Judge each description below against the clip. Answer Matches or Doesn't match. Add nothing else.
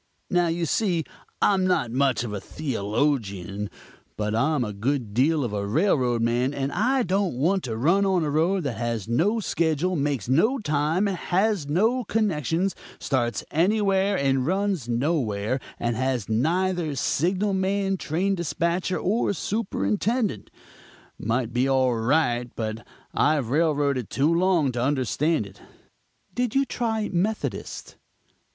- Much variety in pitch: Matches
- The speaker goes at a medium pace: Matches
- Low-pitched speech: Doesn't match